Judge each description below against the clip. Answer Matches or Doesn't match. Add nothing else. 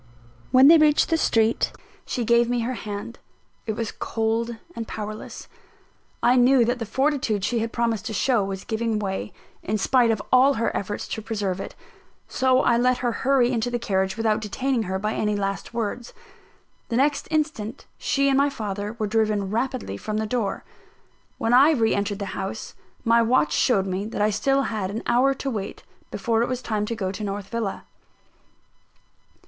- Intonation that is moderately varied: Matches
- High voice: Matches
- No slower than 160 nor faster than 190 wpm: Matches